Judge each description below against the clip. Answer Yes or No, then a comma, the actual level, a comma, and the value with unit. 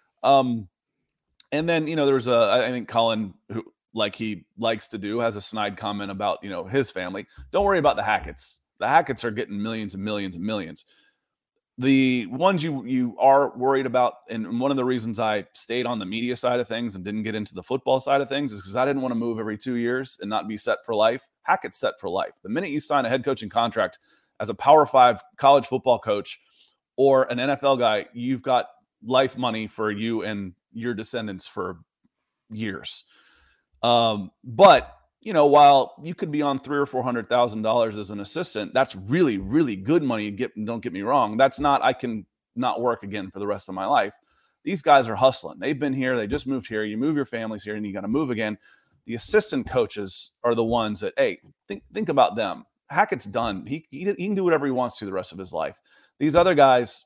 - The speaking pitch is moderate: No, low, 120 Hz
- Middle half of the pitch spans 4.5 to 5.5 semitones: No, average, 4.1 semitones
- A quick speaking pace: Yes, fast, 220 wpm